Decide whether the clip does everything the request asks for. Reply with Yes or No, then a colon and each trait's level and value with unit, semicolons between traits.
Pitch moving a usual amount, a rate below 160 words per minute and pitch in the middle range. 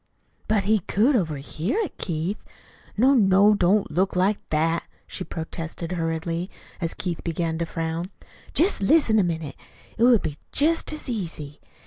Yes: average, 4.6 semitones; average, 150 wpm; medium, 180 Hz